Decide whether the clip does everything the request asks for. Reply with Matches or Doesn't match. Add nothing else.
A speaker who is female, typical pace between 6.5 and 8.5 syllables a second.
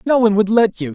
Doesn't match